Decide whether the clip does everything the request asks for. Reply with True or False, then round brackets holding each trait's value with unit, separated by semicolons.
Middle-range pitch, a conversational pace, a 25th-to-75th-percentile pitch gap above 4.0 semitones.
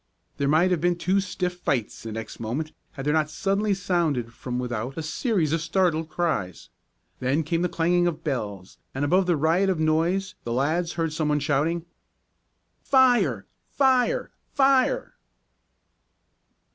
True (165 Hz; 155 wpm; 4.5 semitones)